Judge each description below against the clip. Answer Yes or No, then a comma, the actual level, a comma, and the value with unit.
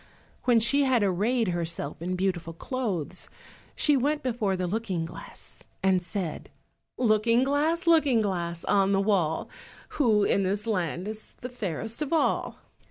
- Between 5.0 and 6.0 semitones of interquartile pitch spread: Yes, wide, 5.5 semitones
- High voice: Yes, high, 210 Hz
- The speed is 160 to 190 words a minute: No, average, 150 wpm